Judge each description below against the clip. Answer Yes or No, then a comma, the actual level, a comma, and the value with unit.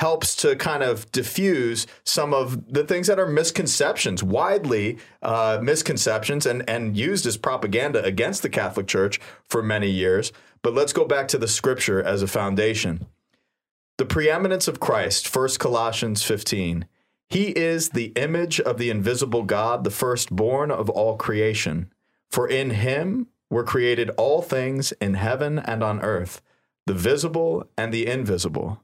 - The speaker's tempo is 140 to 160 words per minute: Yes, average, 155 wpm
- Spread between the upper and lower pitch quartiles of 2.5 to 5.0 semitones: No, wide, 5.5 semitones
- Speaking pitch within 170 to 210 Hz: No, low, 120 Hz